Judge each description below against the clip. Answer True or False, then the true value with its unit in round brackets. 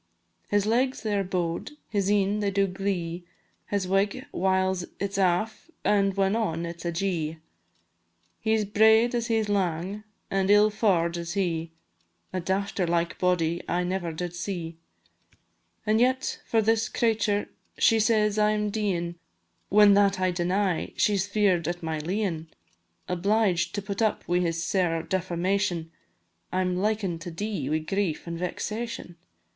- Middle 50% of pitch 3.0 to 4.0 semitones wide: True (3.3 semitones)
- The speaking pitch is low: False (190 Hz)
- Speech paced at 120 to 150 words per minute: False (160 wpm)